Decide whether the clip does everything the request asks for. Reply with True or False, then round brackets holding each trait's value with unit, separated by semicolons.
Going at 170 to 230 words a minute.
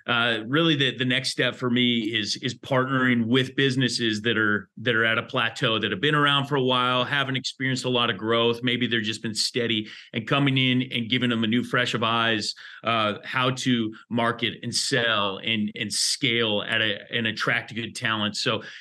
True (205 wpm)